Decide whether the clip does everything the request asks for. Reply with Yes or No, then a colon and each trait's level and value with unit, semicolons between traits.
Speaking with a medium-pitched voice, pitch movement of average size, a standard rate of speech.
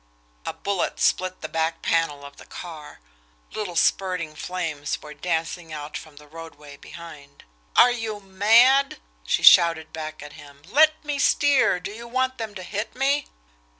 No: medium, 175 Hz; wide, 6.2 semitones; average, 160 wpm